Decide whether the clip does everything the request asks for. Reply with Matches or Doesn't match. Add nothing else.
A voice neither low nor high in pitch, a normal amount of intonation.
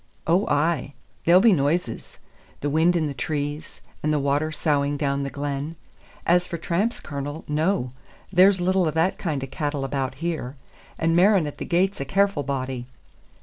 Matches